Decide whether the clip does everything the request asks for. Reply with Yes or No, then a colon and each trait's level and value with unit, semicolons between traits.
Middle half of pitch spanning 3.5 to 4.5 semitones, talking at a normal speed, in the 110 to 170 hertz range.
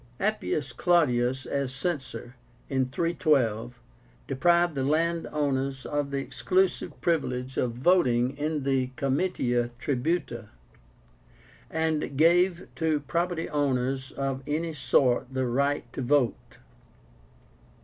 No: average, 3.8 semitones; slow, 105 wpm; medium, 140 Hz